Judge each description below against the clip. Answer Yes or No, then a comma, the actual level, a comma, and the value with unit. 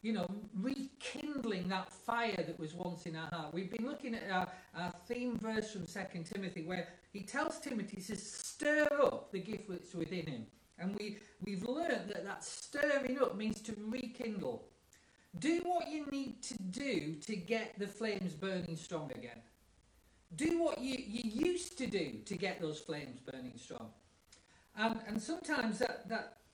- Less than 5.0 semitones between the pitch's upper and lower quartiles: No, wide, 5.6 semitones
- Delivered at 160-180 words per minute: Yes, average, 170 wpm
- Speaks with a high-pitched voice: Yes, high, 210 Hz